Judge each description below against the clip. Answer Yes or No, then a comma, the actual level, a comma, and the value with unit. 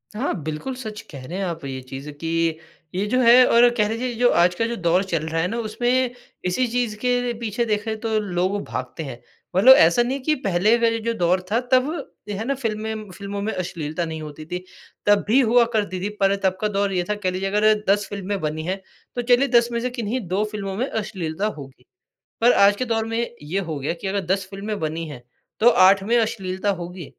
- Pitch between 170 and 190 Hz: No, high, 205 Hz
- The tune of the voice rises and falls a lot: No, average, 4.5 semitones